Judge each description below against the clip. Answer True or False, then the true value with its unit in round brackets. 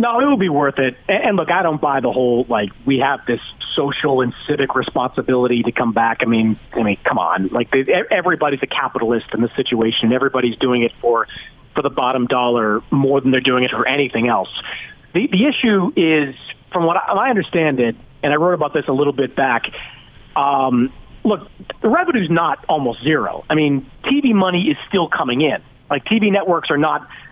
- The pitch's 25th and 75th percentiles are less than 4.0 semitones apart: False (4.5 semitones)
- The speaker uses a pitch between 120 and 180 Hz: True (135 Hz)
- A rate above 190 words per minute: True (200 wpm)